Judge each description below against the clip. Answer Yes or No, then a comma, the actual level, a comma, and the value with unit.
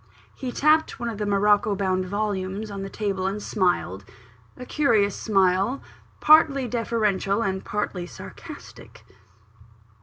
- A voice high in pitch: Yes, high, 205 Hz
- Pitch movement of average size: Yes, average, 3.1 semitones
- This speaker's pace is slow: Yes, slow, 125 wpm